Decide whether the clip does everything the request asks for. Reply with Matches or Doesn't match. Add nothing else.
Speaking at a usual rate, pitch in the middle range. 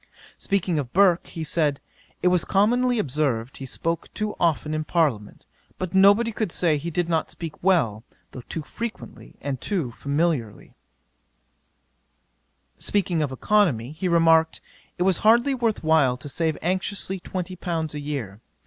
Matches